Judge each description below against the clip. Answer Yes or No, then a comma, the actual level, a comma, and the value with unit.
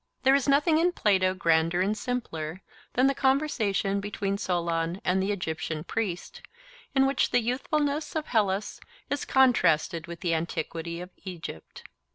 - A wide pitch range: Yes, wide, 7.7 semitones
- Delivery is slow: No, average, 150 wpm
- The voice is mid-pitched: No, high, 195 Hz